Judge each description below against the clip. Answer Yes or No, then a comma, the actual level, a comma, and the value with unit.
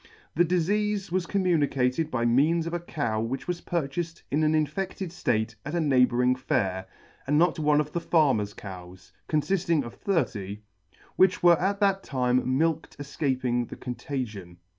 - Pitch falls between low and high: Yes, medium, 150 Hz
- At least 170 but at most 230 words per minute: No, average, 160 wpm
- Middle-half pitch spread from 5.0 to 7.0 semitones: Yes, wide, 5.6 semitones